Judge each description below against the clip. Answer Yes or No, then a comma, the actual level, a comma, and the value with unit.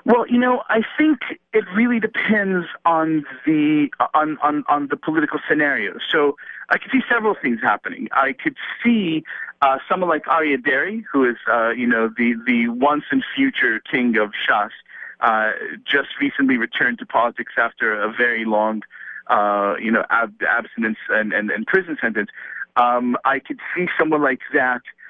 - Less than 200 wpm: Yes, average, 170 wpm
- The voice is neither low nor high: Yes, medium, 155 Hz